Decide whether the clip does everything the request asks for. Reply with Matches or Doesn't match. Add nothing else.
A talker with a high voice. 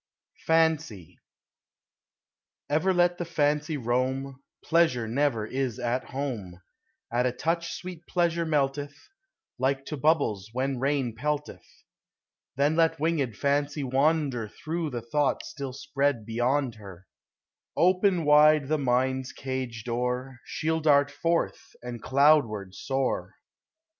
Doesn't match